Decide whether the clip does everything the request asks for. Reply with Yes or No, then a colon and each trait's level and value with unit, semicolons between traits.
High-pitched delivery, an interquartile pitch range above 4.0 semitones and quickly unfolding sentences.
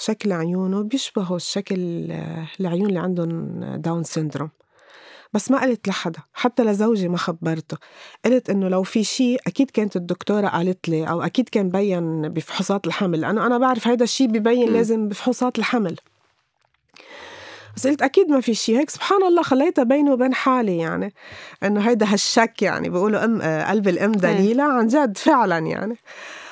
Yes: high, 210 Hz; wide, 5.6 semitones; fast, 155 wpm